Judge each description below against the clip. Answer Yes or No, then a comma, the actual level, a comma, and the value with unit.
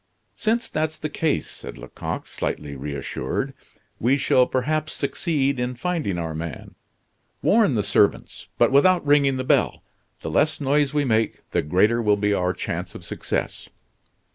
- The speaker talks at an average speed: Yes, average, 155 wpm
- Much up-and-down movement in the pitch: Yes, wide, 6.9 semitones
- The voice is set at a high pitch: No, low, 130 Hz